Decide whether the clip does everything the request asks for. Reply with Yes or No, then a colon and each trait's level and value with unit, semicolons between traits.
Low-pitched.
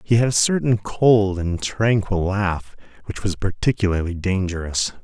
Yes: low, 100 Hz